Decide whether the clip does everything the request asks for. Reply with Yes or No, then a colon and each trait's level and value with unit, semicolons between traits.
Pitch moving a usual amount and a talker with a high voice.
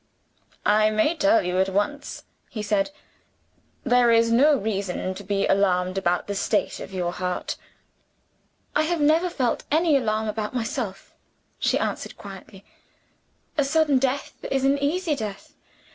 No: wide, 6.4 semitones; high, 225 Hz